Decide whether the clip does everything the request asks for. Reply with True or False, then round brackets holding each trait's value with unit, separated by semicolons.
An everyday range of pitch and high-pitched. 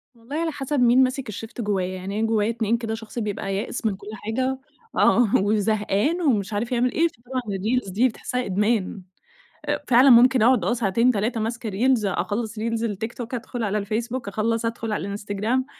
True (3.1 semitones; 225 Hz)